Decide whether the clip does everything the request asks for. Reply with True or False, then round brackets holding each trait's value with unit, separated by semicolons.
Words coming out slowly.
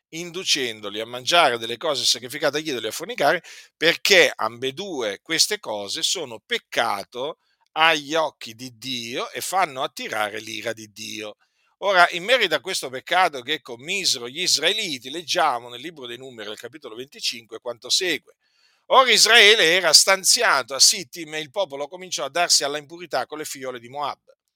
False (160 wpm)